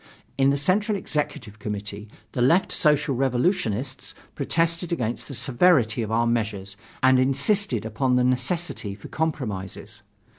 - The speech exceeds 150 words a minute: No, slow, 135 wpm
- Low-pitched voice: Yes, low, 130 Hz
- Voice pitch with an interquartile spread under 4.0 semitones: No, wide, 5.5 semitones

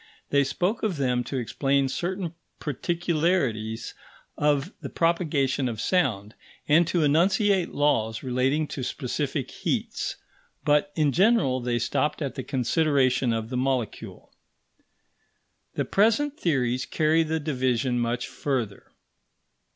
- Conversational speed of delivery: No, slow, 120 wpm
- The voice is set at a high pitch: No, medium, 140 Hz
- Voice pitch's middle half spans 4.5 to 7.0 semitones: Yes, average, 4.8 semitones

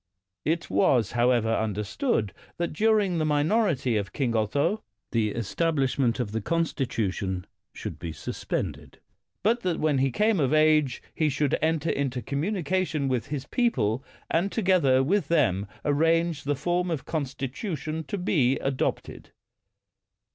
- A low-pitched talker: No, medium, 145 Hz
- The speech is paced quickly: No, average, 140 wpm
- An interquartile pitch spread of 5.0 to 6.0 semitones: Yes, wide, 5.4 semitones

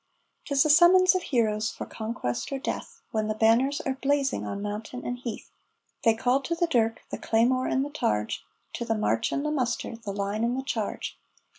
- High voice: Yes, high, 240 Hz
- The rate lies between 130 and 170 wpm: No, average, 200 wpm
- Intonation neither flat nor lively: Yes, average, 4.1 semitones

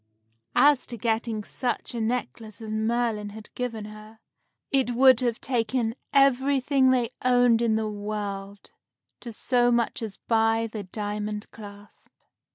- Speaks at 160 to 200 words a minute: No, average, 140 wpm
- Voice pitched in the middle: No, high, 225 Hz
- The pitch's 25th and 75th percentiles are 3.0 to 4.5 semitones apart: No, narrow, 2.6 semitones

